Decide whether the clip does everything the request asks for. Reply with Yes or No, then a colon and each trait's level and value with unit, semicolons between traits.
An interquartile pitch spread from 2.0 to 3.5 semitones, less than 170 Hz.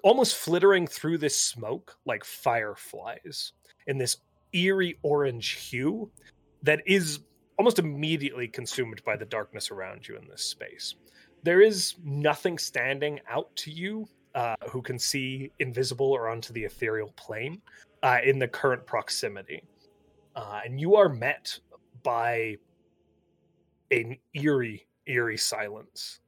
No: average, 5.2 semitones; low, 135 Hz